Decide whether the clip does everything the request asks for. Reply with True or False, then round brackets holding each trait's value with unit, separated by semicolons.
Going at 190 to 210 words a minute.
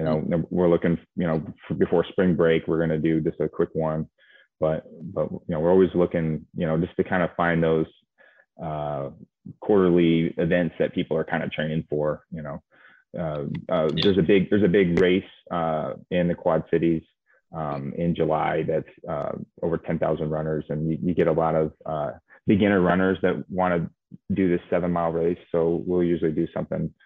True (195 wpm)